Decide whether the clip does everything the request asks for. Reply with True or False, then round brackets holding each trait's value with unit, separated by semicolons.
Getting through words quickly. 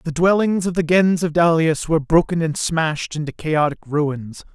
False (185 wpm)